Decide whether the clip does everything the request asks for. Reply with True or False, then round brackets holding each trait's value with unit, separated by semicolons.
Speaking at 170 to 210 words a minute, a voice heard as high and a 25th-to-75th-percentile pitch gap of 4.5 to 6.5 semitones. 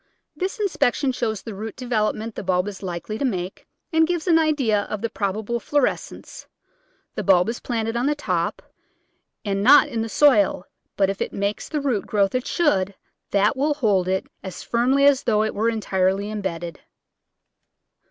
True (175 wpm; 220 Hz; 5.0 semitones)